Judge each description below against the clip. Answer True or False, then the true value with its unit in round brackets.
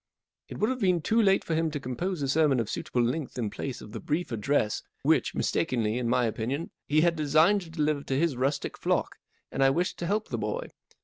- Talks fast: True (220 wpm)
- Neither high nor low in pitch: True (150 Hz)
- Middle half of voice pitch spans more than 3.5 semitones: True (5.5 semitones)